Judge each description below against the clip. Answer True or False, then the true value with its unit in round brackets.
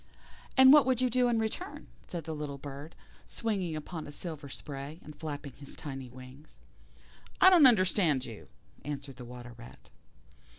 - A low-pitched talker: False (150 Hz)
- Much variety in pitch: True (7.6 semitones)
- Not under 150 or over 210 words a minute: True (165 wpm)